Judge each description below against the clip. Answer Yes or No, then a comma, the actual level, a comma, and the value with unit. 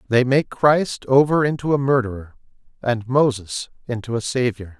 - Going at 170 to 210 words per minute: No, average, 150 wpm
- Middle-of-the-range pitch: No, low, 125 Hz